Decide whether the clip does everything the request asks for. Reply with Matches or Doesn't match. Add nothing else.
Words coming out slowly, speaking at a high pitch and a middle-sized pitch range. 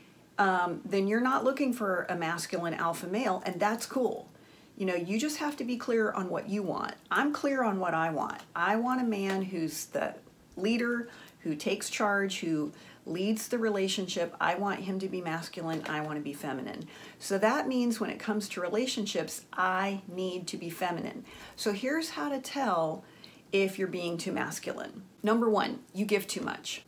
Doesn't match